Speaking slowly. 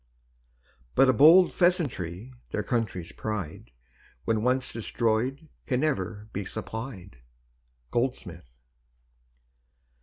Yes: slow, 90 wpm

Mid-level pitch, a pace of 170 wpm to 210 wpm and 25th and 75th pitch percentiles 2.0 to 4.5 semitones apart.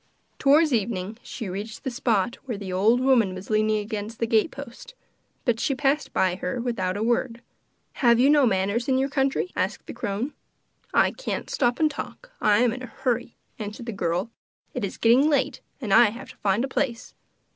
No: high, 235 Hz; average, 200 wpm; average, 4.1 semitones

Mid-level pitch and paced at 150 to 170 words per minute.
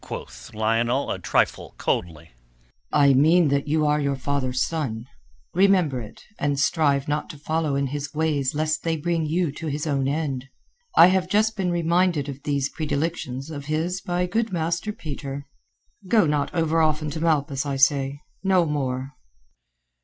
Yes: medium, 150 Hz; average, 165 wpm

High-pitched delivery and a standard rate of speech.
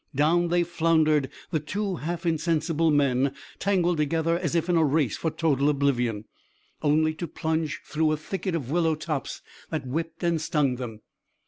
No: medium, 160 Hz; average, 165 wpm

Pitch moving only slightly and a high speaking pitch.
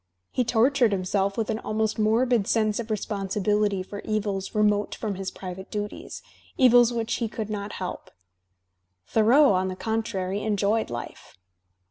Yes: narrow, 2.2 semitones; high, 210 Hz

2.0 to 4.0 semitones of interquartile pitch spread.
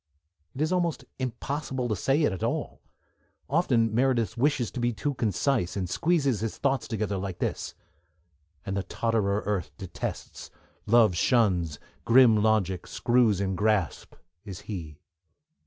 No: average, 4.9 semitones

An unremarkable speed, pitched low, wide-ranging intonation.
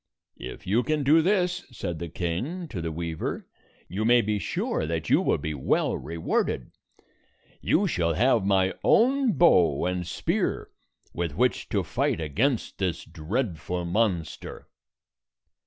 Yes: average, 150 wpm; very low, 90 Hz; wide, 7.1 semitones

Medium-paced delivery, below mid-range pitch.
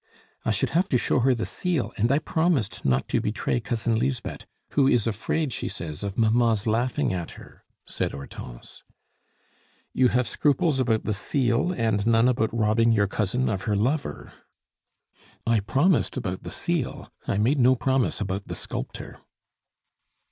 Yes: average, 160 wpm; low, 115 Hz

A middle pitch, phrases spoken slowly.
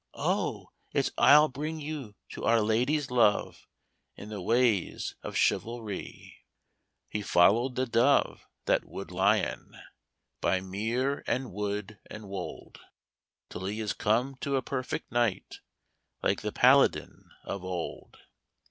No: low, 110 Hz; slow, 130 wpm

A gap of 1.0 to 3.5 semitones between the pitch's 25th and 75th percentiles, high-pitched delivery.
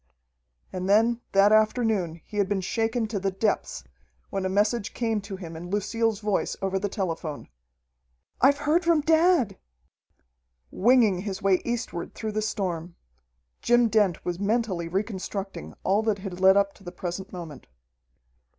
Yes: average, 3.2 semitones; high, 200 Hz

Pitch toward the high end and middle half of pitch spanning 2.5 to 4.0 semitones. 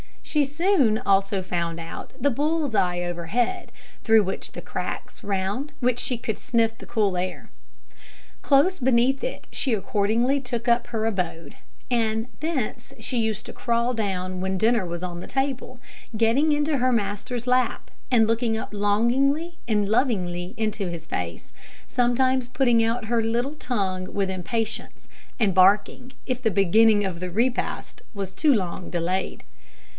No: high, 225 Hz; average, 4.7 semitones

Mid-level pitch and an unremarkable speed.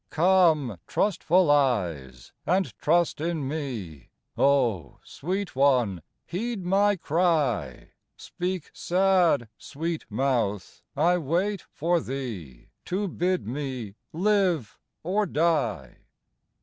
No: medium, 155 Hz; slow, 95 wpm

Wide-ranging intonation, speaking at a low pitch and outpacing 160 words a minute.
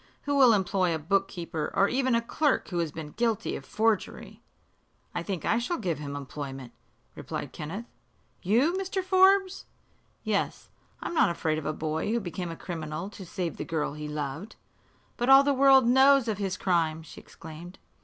No: wide, 7.4 semitones; high, 190 Hz; average, 180 wpm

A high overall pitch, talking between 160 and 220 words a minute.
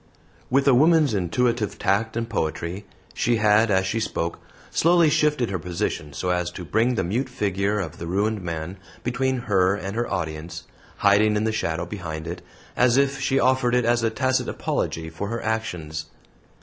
No: low, 105 Hz; average, 180 wpm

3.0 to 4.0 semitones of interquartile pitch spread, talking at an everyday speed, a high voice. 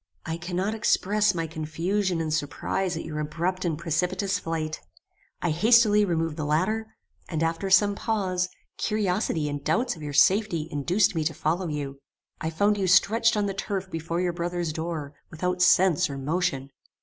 No: average, 3.6 semitones; average, 170 wpm; medium, 175 Hz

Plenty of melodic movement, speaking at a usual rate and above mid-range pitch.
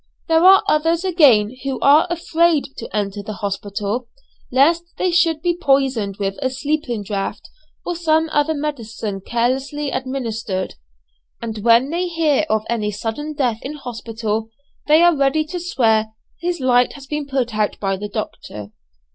Yes: wide, 6.1 semitones; average, 155 wpm; very high, 265 Hz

